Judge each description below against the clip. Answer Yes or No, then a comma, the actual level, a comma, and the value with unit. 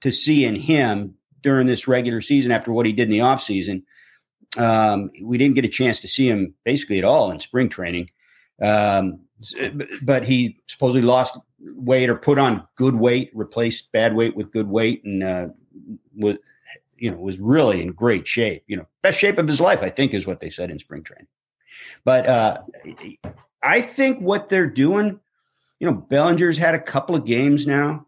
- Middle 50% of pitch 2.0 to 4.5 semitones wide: No, average, 5.1 semitones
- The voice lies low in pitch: Yes, low, 125 Hz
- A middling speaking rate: Yes, average, 190 wpm